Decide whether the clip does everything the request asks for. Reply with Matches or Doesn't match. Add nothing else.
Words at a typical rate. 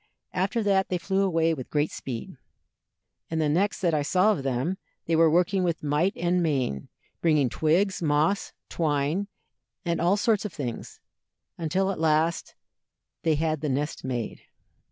Matches